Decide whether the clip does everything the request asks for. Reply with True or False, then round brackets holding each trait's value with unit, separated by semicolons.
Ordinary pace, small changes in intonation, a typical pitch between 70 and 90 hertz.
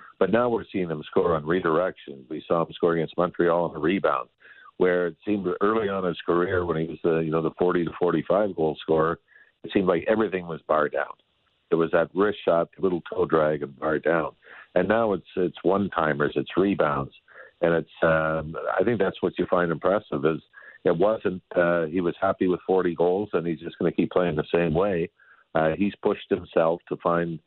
False (220 wpm; 1.9 semitones; 85 Hz)